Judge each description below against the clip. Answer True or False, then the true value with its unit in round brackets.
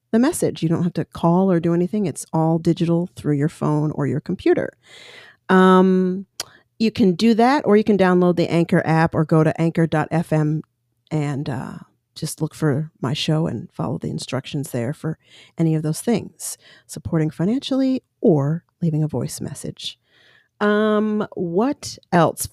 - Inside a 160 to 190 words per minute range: True (165 wpm)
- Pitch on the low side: False (165 Hz)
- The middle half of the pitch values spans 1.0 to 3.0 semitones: False (4.0 semitones)